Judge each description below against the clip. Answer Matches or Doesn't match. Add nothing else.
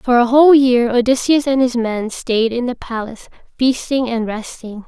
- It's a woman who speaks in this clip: Matches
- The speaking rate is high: Doesn't match